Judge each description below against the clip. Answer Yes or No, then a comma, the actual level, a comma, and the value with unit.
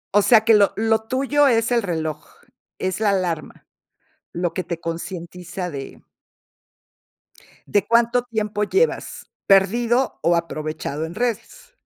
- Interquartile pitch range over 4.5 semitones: Yes, wide, 5.5 semitones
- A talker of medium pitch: No, high, 205 Hz